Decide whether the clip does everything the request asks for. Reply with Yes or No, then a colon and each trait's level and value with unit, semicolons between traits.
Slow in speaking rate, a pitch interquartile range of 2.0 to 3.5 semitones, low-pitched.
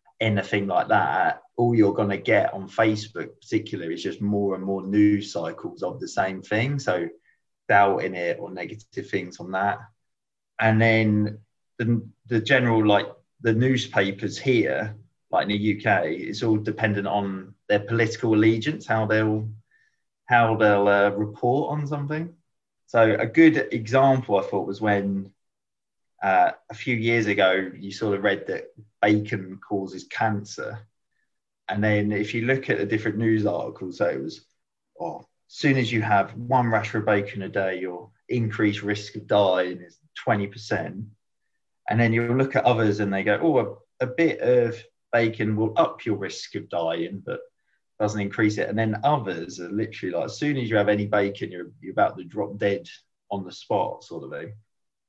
No: average, 180 wpm; narrow, 2.4 semitones; low, 110 Hz